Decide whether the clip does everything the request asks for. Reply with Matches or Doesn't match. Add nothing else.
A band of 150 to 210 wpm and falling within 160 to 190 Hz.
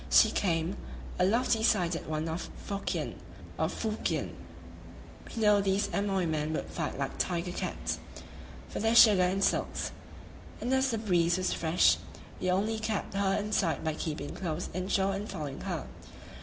Matches